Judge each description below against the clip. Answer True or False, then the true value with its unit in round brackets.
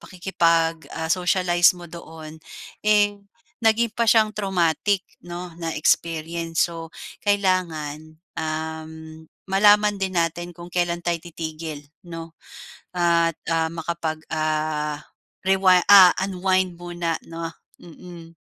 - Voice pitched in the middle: True (170 Hz)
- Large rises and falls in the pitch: False (2.4 semitones)